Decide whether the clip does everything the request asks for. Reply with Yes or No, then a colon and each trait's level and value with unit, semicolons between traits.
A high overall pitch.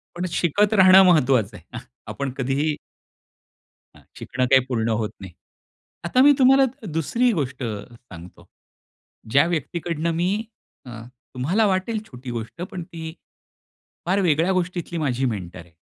No: medium, 155 Hz